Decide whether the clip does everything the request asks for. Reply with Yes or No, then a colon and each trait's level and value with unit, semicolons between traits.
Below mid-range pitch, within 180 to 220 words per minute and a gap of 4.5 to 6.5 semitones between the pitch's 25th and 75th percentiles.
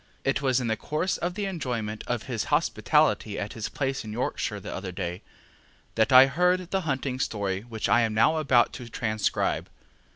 Yes: low, 125 Hz; average, 190 wpm; wide, 5.4 semitones